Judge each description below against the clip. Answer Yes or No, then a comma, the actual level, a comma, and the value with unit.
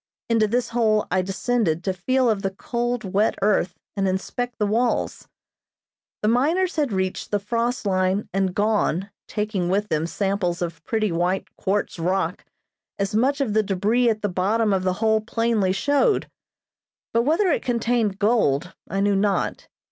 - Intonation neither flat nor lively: Yes, average, 3.7 semitones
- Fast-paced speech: No, average, 165 wpm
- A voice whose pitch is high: Yes, high, 210 Hz